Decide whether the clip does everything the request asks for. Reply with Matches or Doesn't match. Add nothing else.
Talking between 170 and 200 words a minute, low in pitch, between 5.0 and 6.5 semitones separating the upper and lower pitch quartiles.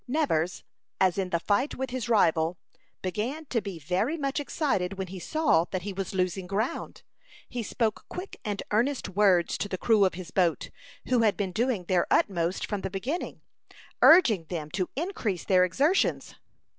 Doesn't match